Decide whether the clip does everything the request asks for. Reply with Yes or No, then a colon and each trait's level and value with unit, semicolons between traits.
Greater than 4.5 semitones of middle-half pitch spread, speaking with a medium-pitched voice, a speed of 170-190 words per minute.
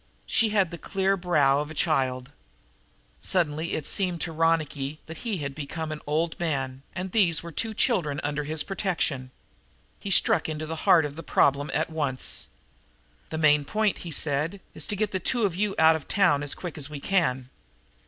No: average, 4.0 semitones; medium, 160 Hz; average, 185 wpm